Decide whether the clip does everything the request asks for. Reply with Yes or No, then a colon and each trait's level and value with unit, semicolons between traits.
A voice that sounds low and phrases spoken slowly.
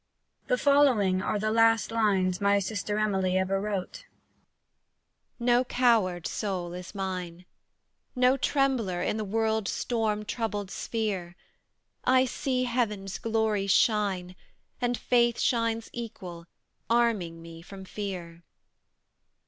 No: high, 210 Hz; slow, 115 wpm